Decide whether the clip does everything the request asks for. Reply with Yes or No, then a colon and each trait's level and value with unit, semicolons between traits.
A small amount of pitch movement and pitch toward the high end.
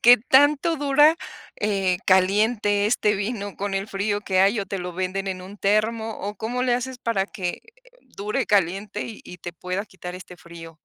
No: average, 3.2 semitones; high, 205 Hz